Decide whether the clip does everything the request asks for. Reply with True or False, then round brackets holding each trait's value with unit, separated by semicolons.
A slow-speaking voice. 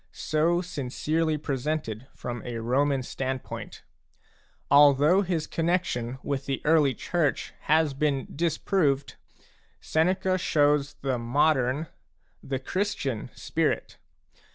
True (100 wpm)